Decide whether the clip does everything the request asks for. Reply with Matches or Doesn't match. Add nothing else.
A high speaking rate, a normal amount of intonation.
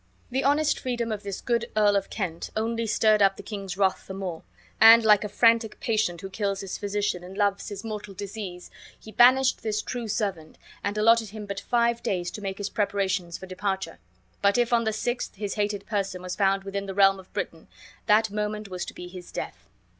Doesn't match